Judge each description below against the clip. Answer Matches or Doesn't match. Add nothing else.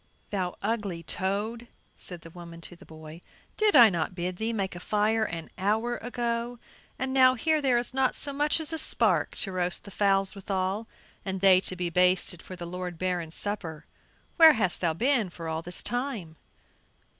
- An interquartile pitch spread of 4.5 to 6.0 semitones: Matches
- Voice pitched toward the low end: Doesn't match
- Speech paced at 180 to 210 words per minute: Matches